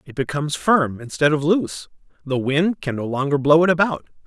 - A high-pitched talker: No, medium, 150 Hz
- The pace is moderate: Yes, average, 195 wpm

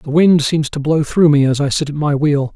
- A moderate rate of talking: No, fast, 305 wpm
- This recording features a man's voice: Yes, male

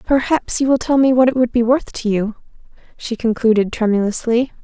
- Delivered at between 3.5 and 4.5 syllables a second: No, 5.4 syllables/s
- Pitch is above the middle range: Yes, high, 240 Hz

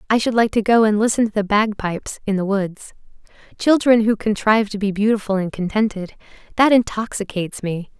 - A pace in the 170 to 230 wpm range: Yes, average, 175 wpm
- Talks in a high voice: Yes, high, 210 Hz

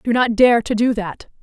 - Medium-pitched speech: No, high, 225 Hz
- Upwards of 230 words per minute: Yes, fast, 250 wpm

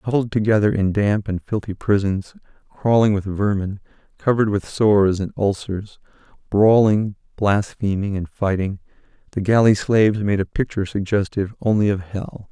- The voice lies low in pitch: Yes, low, 105 Hz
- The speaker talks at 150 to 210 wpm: No, average, 140 wpm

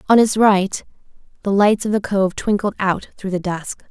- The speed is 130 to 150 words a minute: No, average, 200 wpm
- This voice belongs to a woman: Yes, female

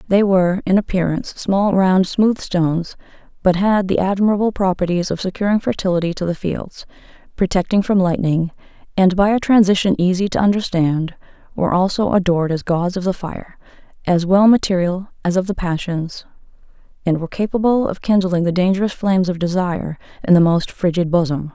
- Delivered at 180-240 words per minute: No, average, 165 wpm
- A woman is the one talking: Yes, female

